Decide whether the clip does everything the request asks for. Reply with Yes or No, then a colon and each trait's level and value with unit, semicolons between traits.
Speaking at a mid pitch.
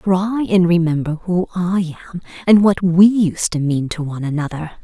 Yes: medium, 175 Hz